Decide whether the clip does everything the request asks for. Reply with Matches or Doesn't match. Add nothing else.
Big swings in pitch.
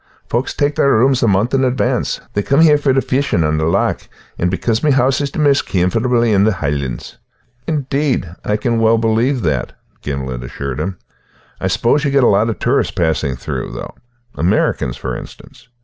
Matches